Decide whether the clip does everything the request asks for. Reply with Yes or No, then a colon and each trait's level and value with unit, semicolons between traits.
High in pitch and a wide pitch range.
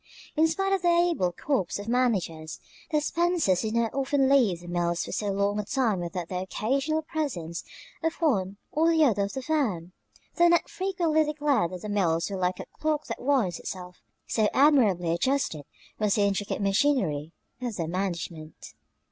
Yes: high, 215 Hz; wide, 8.7 semitones